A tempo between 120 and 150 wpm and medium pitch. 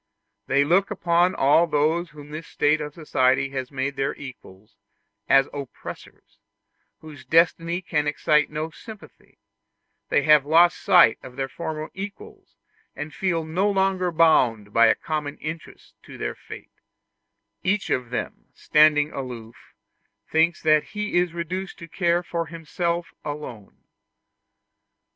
Yes: slow, 135 wpm; medium, 155 Hz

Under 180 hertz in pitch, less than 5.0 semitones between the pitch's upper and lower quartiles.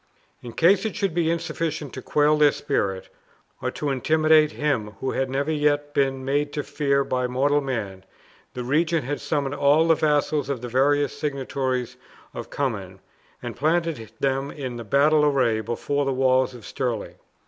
Yes: medium, 140 Hz; average, 2.8 semitones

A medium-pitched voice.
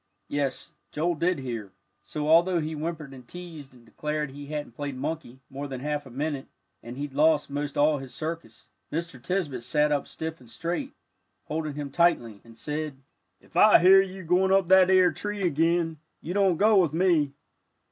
Yes: medium, 150 Hz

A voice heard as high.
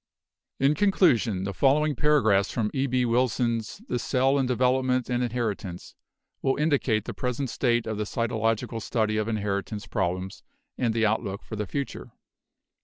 No: low, 120 Hz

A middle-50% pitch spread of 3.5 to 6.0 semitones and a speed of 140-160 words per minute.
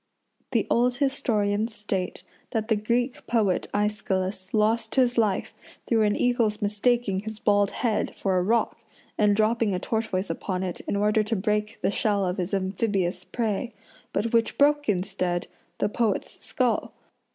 No: average, 2.8 semitones; average, 155 wpm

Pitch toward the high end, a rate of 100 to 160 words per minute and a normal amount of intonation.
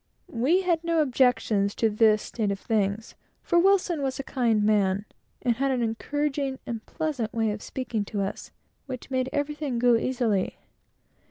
No: high, 245 Hz; average, 170 wpm; average, 4.6 semitones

